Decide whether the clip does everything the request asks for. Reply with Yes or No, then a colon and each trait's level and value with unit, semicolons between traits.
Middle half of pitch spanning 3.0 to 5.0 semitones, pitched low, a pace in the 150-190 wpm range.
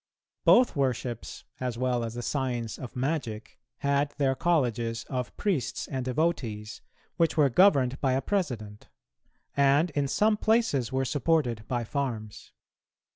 No: average, 3.8 semitones; low, 130 Hz; slow, 135 wpm